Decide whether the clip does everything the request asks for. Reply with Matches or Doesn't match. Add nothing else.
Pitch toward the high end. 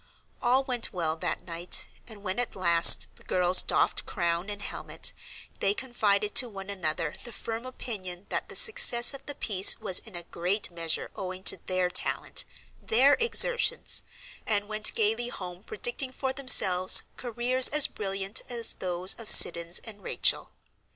Matches